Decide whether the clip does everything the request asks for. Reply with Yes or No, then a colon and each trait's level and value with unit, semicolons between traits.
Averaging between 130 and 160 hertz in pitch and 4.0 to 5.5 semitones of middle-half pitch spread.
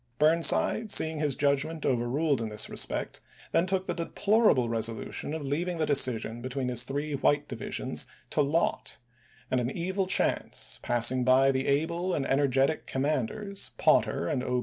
Yes: medium, 140 Hz; average, 4.3 semitones